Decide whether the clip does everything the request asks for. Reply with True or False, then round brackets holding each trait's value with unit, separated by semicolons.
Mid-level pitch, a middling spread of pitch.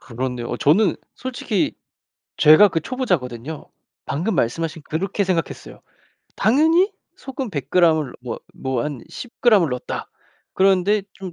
False (175 Hz; 7.5 semitones)